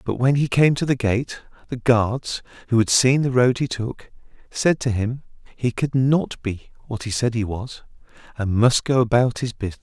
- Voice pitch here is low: Yes, low, 120 Hz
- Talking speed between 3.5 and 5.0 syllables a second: Yes, 4.7 syllables/s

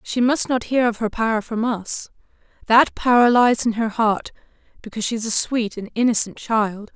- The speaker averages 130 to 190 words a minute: No, average, 200 wpm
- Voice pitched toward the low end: No, high, 225 Hz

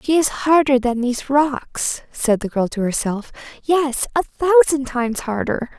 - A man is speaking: No, female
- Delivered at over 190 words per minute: No, average, 165 wpm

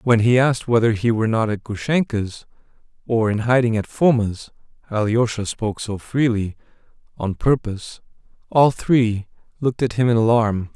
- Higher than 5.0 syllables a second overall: Yes, 5.5 syllables/s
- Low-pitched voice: Yes, low, 115 Hz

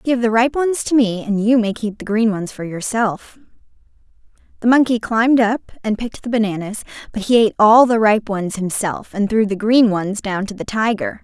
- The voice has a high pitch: Yes, high, 220 Hz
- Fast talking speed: Yes, fast, 215 wpm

